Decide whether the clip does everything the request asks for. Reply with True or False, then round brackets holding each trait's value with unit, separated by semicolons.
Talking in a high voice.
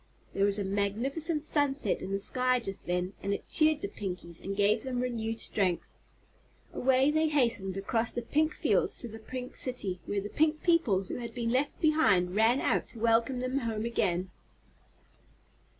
True (230 Hz)